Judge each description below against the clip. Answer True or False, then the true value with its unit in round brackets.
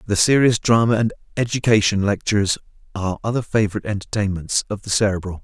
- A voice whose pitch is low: True (105 Hz)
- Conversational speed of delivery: True (145 wpm)